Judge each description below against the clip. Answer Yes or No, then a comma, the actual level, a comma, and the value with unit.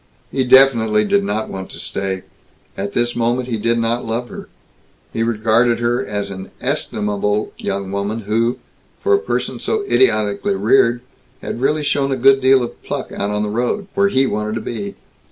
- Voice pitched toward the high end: No, low, 115 Hz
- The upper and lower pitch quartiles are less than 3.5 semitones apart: No, average, 3.9 semitones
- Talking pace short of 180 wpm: No, average, 185 wpm